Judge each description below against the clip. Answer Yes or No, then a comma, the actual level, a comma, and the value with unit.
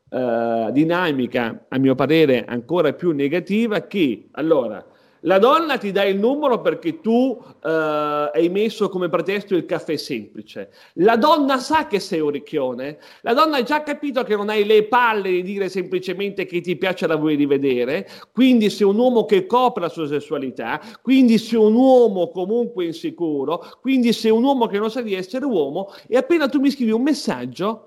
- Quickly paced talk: Yes, fast, 180 wpm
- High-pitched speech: Yes, high, 200 Hz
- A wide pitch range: Yes, wide, 7.3 semitones